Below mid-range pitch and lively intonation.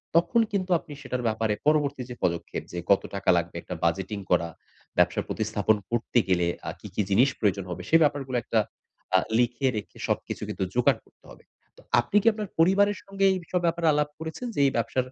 Yes: low, 125 Hz; wide, 8.3 semitones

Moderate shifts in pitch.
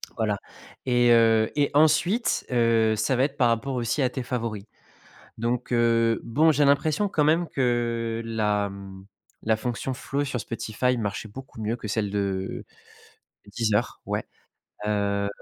Yes: average, 3.2 semitones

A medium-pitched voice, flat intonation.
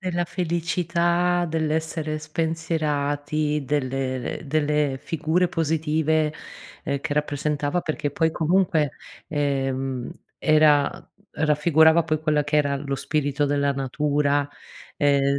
Yes: medium, 150 Hz; narrow, 2.0 semitones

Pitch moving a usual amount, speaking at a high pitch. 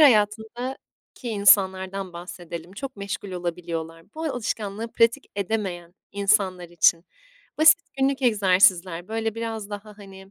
Yes: average, 3.7 semitones; high, 200 Hz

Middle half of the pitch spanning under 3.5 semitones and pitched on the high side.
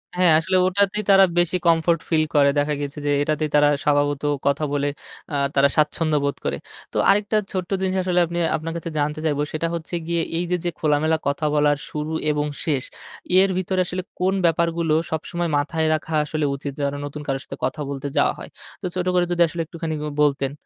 No: average, 3.0 semitones; medium, 155 Hz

